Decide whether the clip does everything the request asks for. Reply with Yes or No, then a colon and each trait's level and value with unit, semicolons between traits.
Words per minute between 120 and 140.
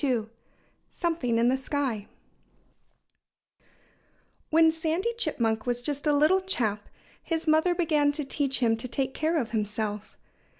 Yes: slow, 135 wpm